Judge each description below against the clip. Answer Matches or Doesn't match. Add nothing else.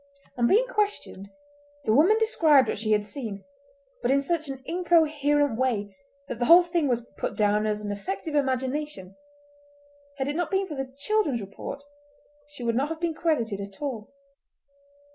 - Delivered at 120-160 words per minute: Doesn't match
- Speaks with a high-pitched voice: Matches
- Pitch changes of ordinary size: Doesn't match